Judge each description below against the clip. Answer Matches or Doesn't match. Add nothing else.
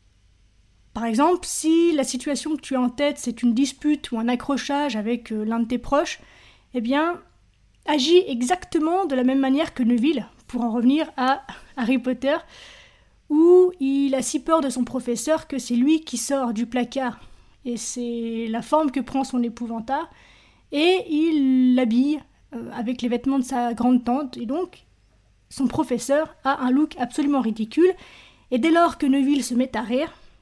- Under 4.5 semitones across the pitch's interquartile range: Matches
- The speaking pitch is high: Matches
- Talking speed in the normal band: Matches